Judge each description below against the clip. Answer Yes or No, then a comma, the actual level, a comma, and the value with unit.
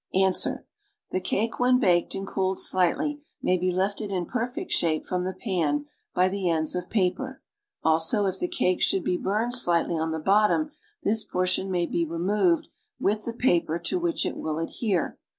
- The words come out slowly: No, average, 185 wpm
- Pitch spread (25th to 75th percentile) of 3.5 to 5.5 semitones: Yes, average, 4.0 semitones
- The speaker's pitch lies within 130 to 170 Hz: No, medium, 185 Hz